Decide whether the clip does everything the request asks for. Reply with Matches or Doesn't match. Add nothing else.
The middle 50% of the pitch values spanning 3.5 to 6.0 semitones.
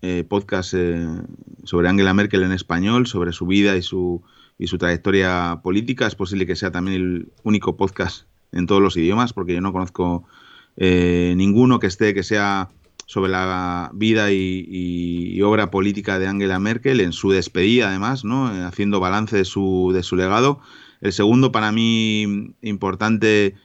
Doesn't match